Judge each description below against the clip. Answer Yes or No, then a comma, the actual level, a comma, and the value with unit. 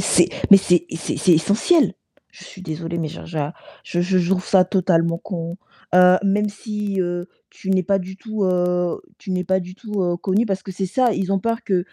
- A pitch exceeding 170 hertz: Yes, medium, 185 Hz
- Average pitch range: No, narrow, 2.1 semitones